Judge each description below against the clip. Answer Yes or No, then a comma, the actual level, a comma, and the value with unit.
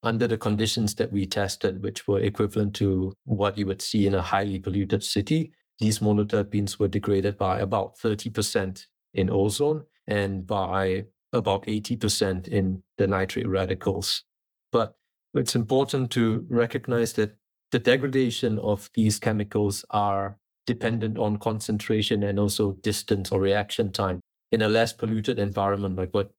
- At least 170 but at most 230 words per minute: No, average, 145 wpm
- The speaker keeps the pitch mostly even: Yes, narrow, 2.3 semitones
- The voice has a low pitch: Yes, low, 105 Hz